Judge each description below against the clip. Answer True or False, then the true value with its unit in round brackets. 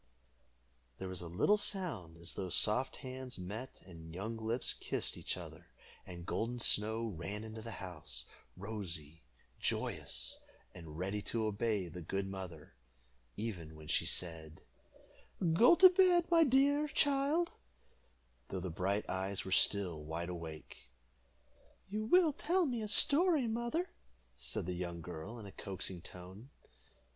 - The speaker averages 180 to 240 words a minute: False (145 wpm)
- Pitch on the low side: True (100 Hz)